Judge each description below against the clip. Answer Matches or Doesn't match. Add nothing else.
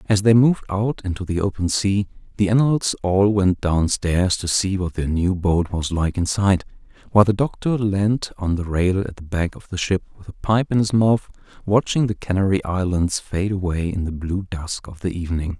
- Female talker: Doesn't match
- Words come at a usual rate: Doesn't match